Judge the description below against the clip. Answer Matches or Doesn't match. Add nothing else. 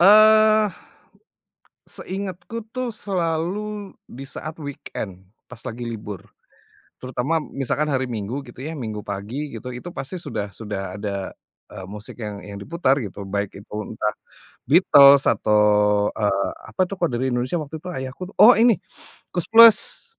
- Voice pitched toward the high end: Doesn't match